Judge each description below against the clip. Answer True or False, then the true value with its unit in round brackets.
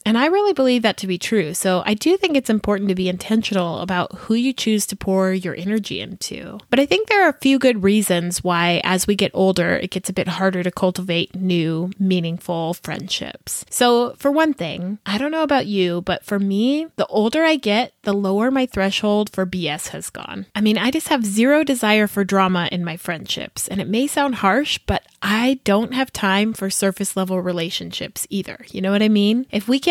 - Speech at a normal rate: False (215 wpm)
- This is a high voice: True (200 Hz)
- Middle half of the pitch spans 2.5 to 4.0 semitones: False (4.7 semitones)